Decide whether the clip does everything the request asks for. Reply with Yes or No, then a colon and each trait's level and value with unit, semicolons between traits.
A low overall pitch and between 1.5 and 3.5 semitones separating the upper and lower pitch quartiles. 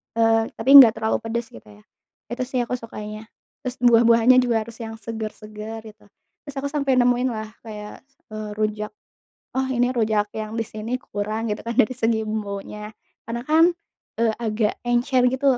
No: high, 225 Hz; narrow, 2.4 semitones